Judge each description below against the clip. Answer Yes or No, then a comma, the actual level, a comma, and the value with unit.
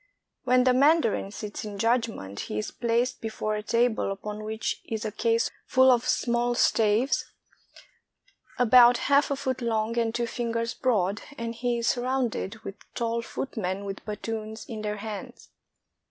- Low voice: No, high, 230 Hz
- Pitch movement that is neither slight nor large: No, narrow, 2.2 semitones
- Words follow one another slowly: No, average, 170 wpm